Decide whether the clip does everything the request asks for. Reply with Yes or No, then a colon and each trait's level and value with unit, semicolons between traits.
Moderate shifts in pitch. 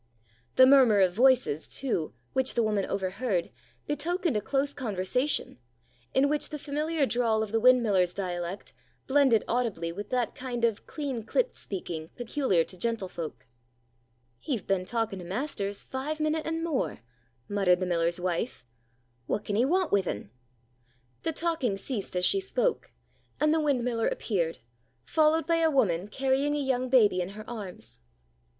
No: wide, 6.7 semitones